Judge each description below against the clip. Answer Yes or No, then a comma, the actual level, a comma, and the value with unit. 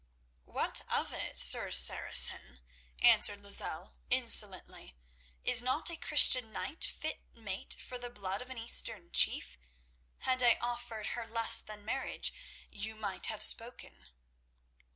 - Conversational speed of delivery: No, slow, 130 wpm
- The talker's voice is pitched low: No, high, 225 Hz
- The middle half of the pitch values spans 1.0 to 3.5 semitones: Yes, average, 3.2 semitones